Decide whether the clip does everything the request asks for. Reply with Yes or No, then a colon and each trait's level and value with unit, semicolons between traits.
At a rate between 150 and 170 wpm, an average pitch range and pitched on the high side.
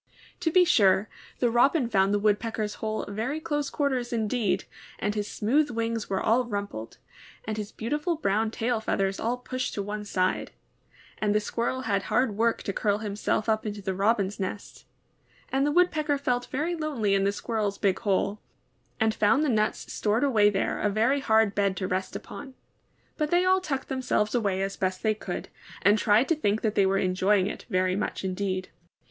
No: average, 190 wpm; average, 4.0 semitones; high, 215 Hz